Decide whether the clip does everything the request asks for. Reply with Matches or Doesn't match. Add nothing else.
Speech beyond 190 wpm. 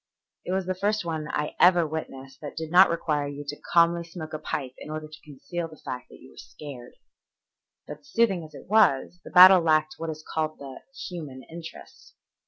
Matches